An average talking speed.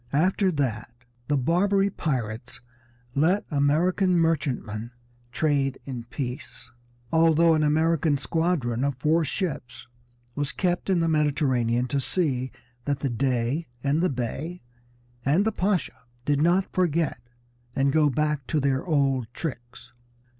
No: slow, 130 wpm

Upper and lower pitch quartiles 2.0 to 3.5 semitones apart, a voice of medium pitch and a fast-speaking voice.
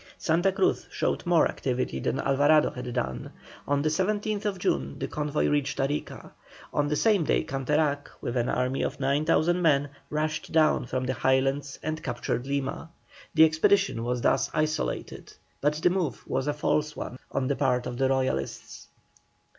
No: average, 3.1 semitones; medium, 145 Hz; average, 165 wpm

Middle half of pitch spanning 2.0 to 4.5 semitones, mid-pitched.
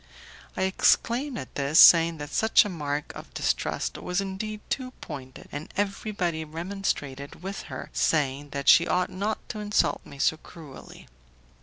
No: wide, 5.4 semitones; medium, 170 Hz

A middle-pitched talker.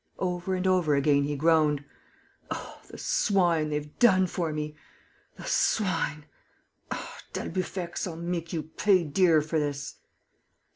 Yes: medium, 165 Hz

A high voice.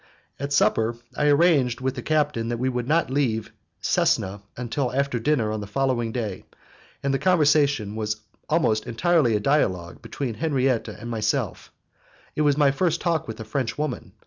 No: low, 130 Hz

